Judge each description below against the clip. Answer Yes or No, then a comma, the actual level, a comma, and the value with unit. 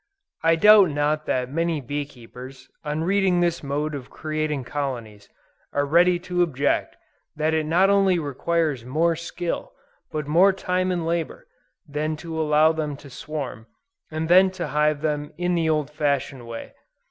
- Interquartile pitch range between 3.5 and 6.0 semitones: No, average, 3.0 semitones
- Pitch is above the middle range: No, medium, 155 Hz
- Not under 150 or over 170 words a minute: Yes, average, 160 wpm